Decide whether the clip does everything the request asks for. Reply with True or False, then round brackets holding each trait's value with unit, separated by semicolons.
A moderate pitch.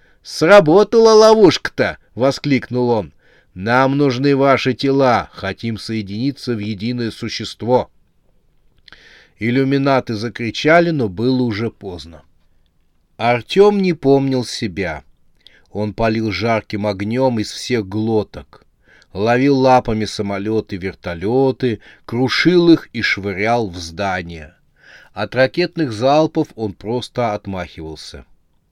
False (115 Hz)